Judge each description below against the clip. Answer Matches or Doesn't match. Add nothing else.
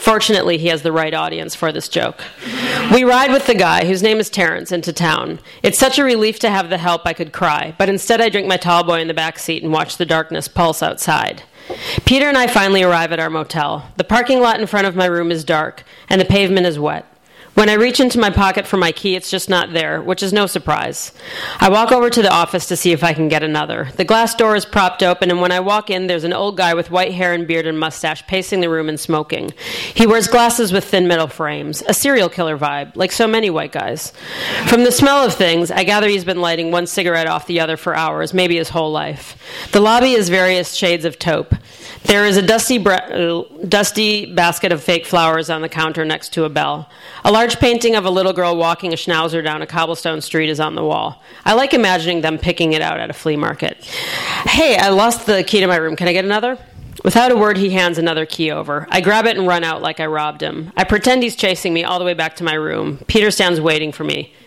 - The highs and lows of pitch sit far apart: Doesn't match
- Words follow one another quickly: Matches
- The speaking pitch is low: Doesn't match